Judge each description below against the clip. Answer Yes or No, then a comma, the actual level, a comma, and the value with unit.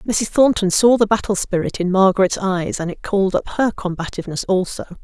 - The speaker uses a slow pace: No, average, 190 wpm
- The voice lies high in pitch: Yes, high, 195 Hz